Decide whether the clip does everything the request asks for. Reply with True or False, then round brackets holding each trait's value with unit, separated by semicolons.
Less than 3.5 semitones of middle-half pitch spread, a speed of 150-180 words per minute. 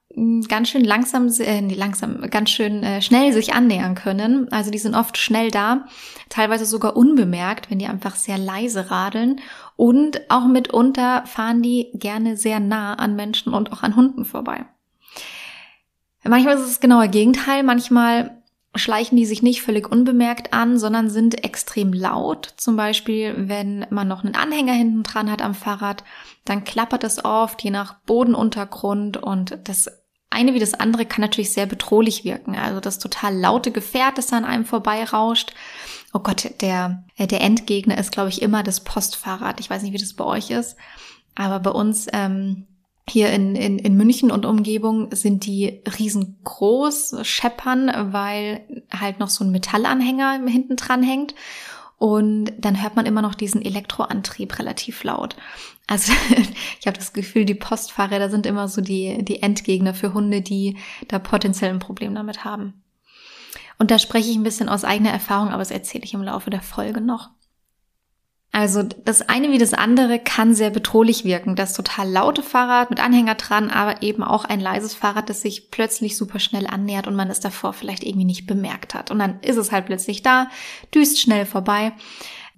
True (2.7 semitones; 175 wpm)